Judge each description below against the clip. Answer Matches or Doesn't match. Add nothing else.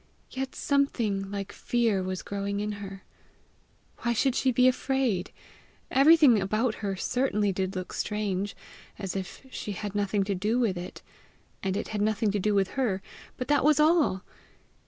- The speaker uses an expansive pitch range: Doesn't match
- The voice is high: Matches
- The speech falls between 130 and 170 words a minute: Matches